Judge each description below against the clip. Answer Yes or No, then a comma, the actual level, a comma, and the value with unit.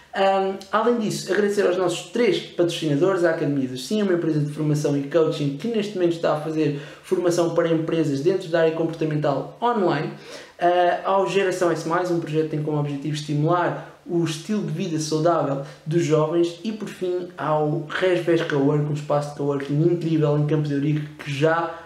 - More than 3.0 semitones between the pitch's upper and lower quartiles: No, average, 2.7 semitones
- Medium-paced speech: Yes, average, 185 wpm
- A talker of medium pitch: Yes, medium, 165 Hz